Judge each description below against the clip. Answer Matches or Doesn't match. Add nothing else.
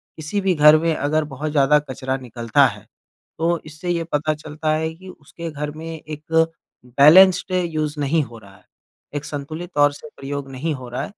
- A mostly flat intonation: Matches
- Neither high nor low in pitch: Matches